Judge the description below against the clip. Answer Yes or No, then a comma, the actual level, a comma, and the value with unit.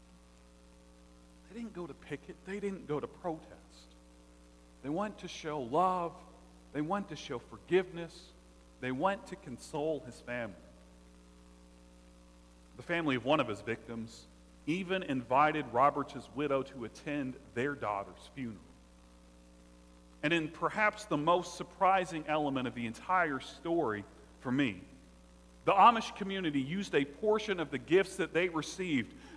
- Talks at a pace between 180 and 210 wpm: No, slow, 135 wpm